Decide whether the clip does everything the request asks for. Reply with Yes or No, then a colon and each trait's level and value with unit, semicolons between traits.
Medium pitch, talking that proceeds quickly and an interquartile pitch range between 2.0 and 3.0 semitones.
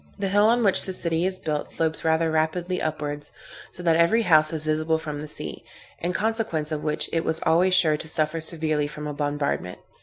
Yes: medium, 160 Hz; fast, 210 wpm; narrow, 2.6 semitones